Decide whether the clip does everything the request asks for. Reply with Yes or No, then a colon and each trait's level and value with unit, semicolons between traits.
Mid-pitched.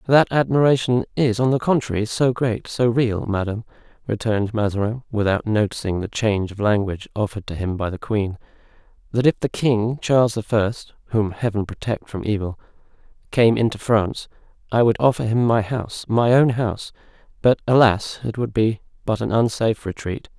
No: low, 110 Hz